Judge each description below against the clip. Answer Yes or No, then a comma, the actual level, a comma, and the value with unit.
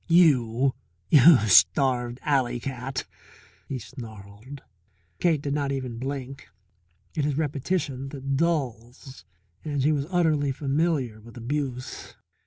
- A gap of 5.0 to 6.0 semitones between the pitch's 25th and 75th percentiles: No, average, 3.0 semitones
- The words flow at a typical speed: No, slow, 110 wpm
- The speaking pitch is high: No, low, 135 Hz